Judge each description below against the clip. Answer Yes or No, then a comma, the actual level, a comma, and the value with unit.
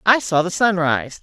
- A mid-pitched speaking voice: Yes, medium, 175 Hz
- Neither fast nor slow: No, fast, 245 wpm